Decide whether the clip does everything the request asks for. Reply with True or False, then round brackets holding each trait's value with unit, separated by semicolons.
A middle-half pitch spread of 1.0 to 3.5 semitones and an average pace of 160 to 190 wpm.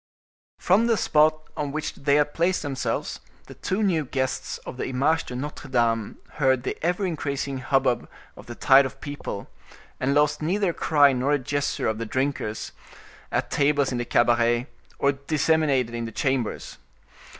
True (3.2 semitones; 170 wpm)